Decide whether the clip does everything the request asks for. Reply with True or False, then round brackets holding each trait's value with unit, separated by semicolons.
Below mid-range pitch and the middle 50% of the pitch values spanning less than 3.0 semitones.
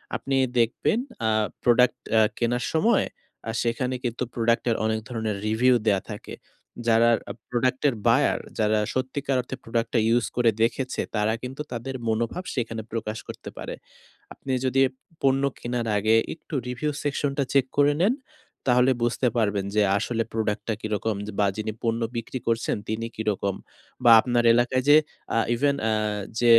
True (120 Hz; 2.6 semitones)